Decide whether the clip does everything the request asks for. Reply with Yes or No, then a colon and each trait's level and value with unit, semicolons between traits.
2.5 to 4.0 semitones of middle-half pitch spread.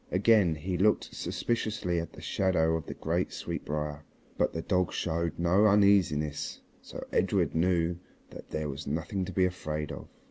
Yes: average, 3.4 semitones